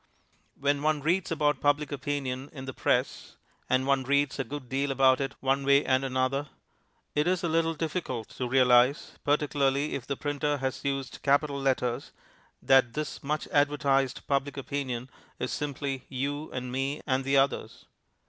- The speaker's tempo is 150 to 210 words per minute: Yes, average, 165 wpm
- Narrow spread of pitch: Yes, narrow, 1.7 semitones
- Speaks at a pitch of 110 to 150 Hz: Yes, medium, 140 Hz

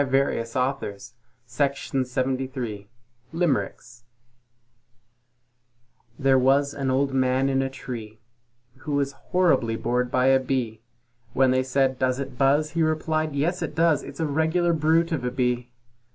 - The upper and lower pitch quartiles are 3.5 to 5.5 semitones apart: No, average, 2.8 semitones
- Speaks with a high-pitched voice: No, low, 135 Hz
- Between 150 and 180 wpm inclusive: No, average, 140 wpm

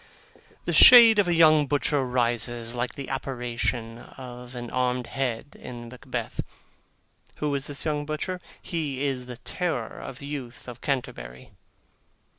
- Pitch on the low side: Yes, low, 130 Hz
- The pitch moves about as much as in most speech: Yes, average, 3.3 semitones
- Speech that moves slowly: No, average, 145 wpm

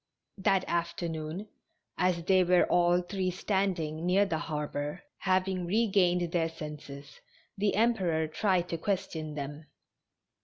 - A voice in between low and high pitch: Yes, medium, 175 Hz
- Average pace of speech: No, slow, 120 wpm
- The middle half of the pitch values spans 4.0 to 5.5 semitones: No, average, 3.2 semitones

